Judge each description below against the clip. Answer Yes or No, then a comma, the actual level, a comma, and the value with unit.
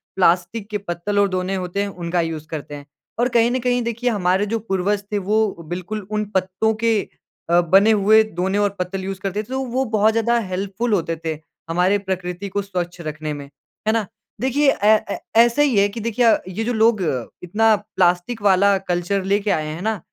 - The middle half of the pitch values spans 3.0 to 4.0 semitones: Yes, average, 3.5 semitones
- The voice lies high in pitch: Yes, high, 200 Hz